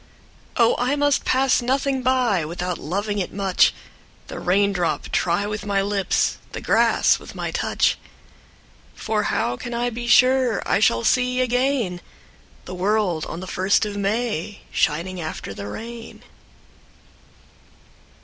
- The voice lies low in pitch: No, high, 205 Hz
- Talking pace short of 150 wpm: Yes, average, 140 wpm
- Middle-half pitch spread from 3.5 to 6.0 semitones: Yes, average, 5.2 semitones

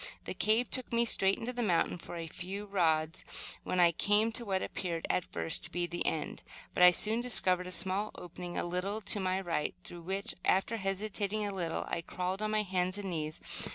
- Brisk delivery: Yes, fast, 215 wpm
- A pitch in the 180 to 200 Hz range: Yes, high, 190 Hz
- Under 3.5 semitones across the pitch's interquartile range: Yes, average, 3.1 semitones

